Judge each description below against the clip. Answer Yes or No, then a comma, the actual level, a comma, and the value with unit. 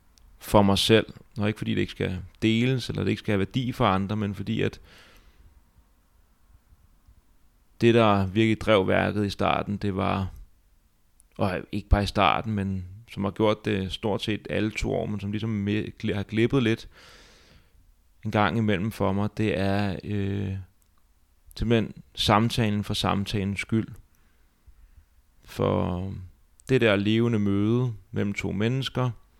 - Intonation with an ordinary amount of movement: Yes, average, 3.7 semitones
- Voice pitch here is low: Yes, low, 100 Hz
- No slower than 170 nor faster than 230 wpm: No, slow, 145 wpm